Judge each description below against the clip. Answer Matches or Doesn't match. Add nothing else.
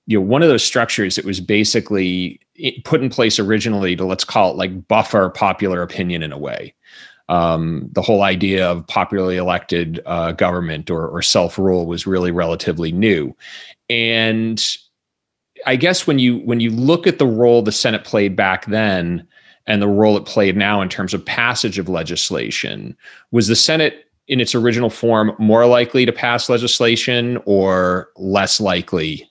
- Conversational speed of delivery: Matches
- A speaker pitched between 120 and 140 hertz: Doesn't match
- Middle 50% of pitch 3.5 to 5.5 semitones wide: Matches